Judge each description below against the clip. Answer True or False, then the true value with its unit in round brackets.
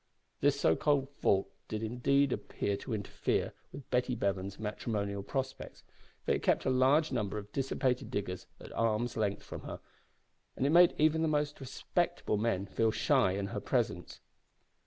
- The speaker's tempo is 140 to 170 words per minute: True (165 wpm)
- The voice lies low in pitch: True (115 Hz)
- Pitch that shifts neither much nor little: True (5.0 semitones)